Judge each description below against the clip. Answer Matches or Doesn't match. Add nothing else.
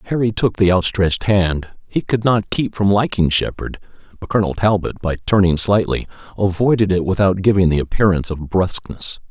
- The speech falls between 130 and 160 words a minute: Matches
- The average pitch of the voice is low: Matches